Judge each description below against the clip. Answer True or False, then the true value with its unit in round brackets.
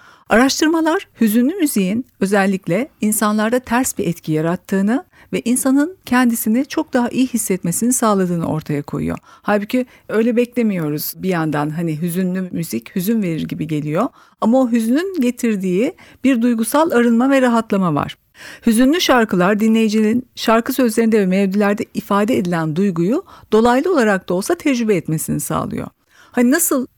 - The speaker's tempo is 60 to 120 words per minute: False (135 wpm)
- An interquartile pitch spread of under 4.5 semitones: False (5.2 semitones)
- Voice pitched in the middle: False (225 Hz)